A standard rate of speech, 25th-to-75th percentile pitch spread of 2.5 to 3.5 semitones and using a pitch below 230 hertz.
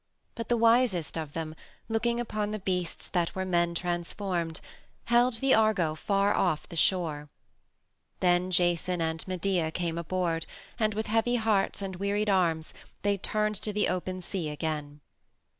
No: average, 155 wpm; average, 4.0 semitones; medium, 185 Hz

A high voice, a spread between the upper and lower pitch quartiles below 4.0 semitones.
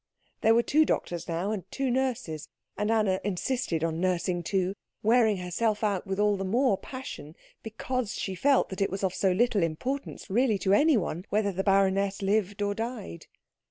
Yes: high, 200 Hz; average, 3.6 semitones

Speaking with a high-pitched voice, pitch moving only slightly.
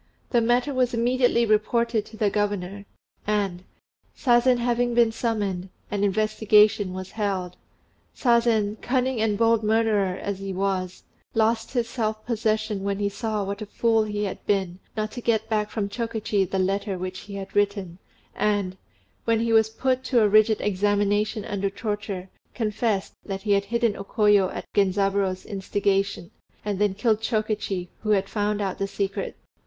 Yes: high, 210 Hz; narrow, 2.3 semitones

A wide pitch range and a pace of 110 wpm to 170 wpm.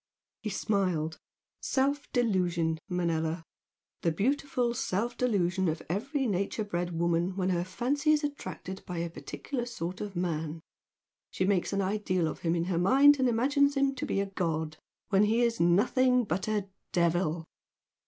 Yes: wide, 5.9 semitones; average, 160 wpm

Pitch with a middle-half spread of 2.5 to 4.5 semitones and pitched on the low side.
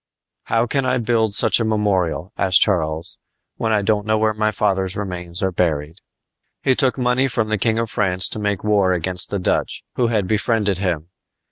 Yes: average, 3.4 semitones; low, 105 Hz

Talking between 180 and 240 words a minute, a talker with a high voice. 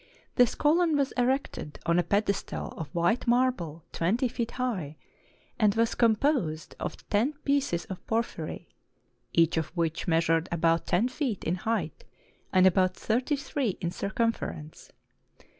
No: average, 145 wpm; high, 205 Hz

